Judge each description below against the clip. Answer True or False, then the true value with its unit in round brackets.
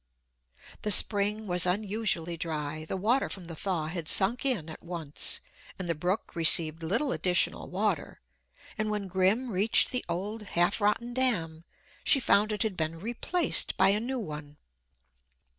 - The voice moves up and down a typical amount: True (4.5 semitones)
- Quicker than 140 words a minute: True (160 wpm)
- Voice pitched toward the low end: False (190 Hz)